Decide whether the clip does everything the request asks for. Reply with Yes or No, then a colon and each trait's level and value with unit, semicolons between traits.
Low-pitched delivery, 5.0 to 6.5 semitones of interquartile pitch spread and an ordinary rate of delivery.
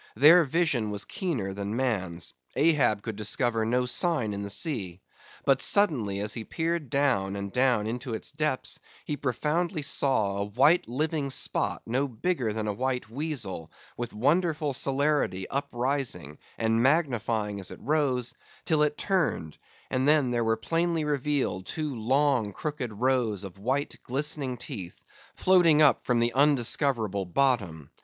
Yes: low, 125 Hz; wide, 5.6 semitones; average, 150 wpm